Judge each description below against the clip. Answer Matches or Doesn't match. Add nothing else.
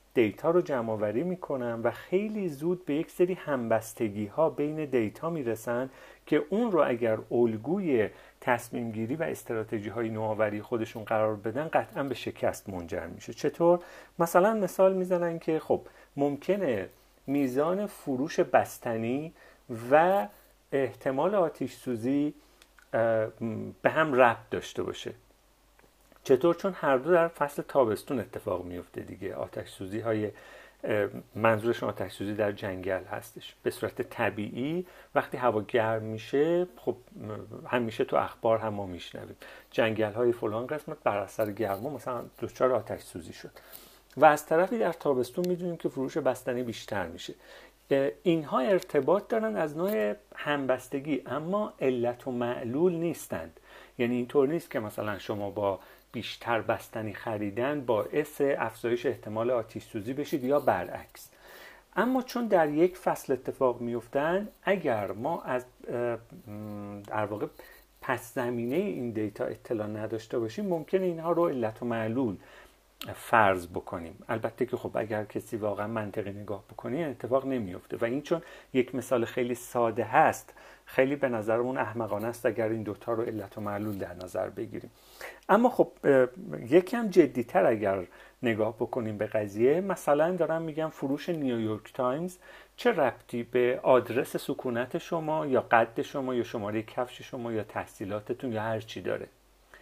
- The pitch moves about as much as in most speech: Doesn't match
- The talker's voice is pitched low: Matches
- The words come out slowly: Doesn't match